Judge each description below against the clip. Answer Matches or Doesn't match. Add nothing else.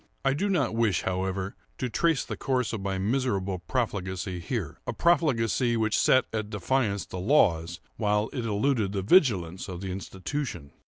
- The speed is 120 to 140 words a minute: Doesn't match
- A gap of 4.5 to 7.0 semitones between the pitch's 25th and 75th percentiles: Matches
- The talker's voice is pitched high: Doesn't match